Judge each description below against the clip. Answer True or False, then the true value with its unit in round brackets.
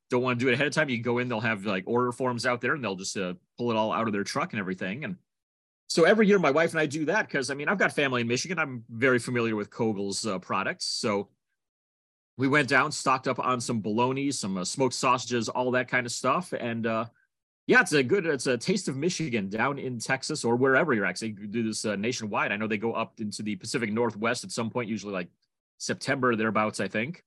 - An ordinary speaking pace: False (260 wpm)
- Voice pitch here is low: True (120 Hz)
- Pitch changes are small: False (3.3 semitones)